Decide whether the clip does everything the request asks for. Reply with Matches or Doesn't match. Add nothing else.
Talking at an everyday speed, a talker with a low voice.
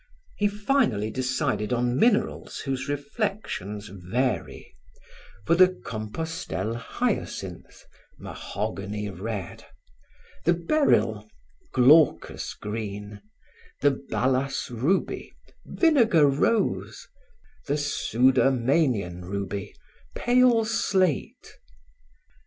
Doesn't match